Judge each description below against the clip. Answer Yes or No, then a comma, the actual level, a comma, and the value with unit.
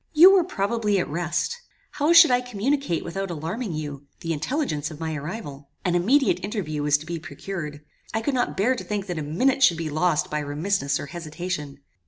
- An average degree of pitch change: No, wide, 7.1 semitones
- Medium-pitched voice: Yes, medium, 175 Hz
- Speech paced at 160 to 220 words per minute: Yes, average, 200 wpm